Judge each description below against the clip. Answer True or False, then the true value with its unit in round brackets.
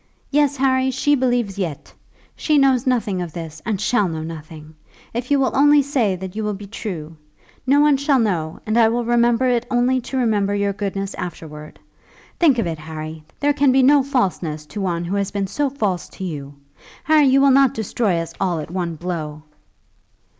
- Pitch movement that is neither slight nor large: False (7.3 semitones)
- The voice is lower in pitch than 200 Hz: False (210 Hz)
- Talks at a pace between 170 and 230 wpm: True (195 wpm)